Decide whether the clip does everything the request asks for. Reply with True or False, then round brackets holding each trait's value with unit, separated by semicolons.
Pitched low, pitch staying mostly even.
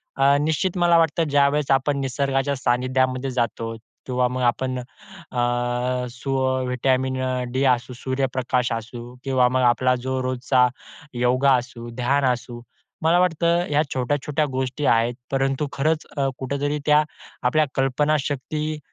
True (130 Hz; 2.3 semitones)